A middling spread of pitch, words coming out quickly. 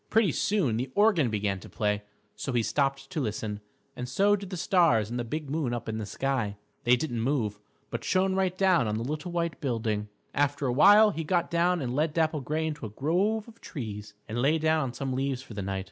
No: wide, 6.6 semitones; fast, 230 wpm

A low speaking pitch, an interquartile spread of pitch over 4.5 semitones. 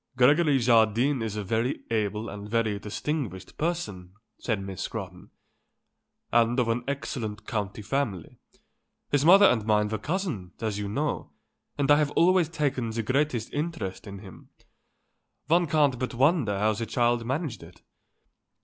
Yes: low, 115 Hz; wide, 5.5 semitones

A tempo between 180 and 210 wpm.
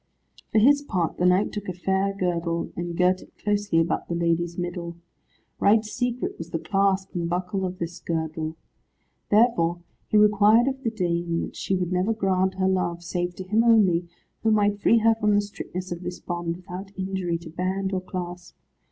Yes: average, 190 wpm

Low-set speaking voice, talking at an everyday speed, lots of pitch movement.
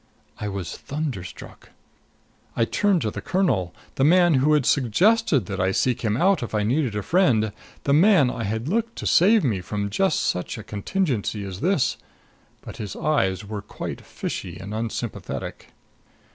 Yes: low, 120 Hz; average, 175 wpm; wide, 8.4 semitones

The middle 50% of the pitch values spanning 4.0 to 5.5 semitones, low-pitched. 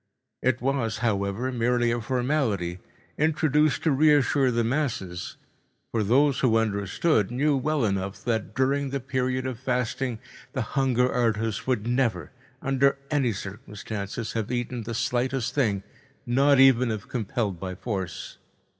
No: average, 3.6 semitones; low, 125 Hz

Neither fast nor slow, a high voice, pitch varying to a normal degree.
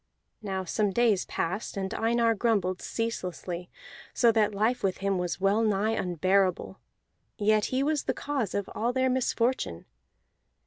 Yes: average, 145 wpm; high, 210 Hz; average, 3.5 semitones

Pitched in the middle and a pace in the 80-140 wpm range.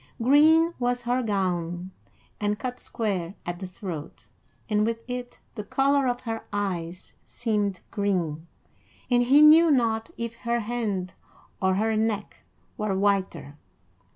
No: high, 215 Hz; slow, 135 wpm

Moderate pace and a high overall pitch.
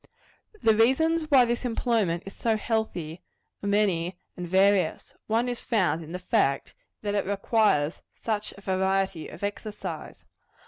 Yes: average, 145 wpm; high, 200 Hz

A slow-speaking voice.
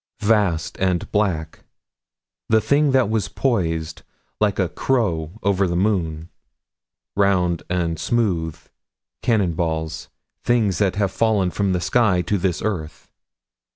Yes: slow, 130 wpm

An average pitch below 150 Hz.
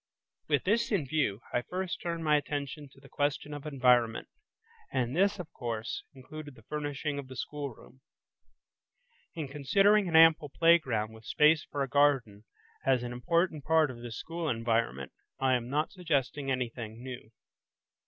Yes: medium, 140 Hz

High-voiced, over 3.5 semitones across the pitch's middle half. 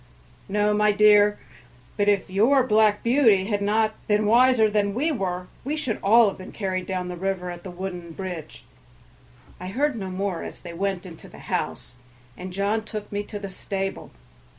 No: high, 205 Hz; narrow, 2.5 semitones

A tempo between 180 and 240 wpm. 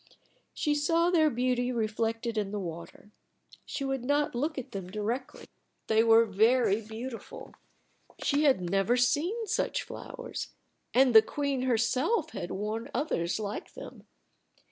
No: average, 140 wpm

